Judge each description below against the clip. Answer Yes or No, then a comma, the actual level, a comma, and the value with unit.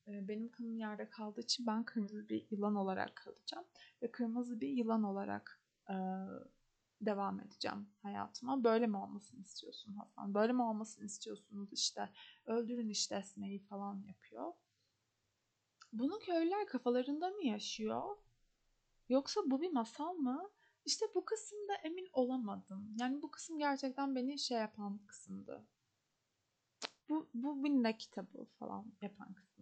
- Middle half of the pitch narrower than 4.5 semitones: No, average, 5.2 semitones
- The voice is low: No, high, 230 Hz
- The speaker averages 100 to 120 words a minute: No, average, 130 wpm